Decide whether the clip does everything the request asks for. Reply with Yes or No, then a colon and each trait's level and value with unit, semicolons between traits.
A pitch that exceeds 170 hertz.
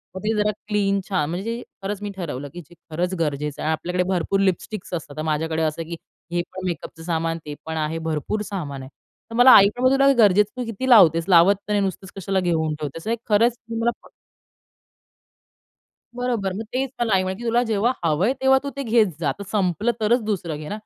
Yes: high, 190 Hz